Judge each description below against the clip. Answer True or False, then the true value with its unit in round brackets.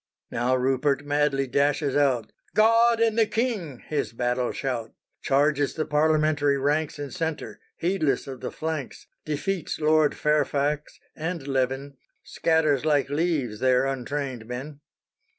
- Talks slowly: True (130 wpm)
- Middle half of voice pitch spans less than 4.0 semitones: True (2.7 semitones)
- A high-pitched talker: False (145 Hz)